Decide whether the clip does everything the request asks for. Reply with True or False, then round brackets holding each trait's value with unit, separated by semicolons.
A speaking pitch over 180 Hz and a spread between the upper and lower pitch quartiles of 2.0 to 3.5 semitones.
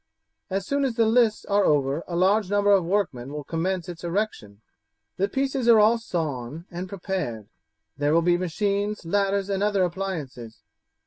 False (190 Hz; 3.9 semitones)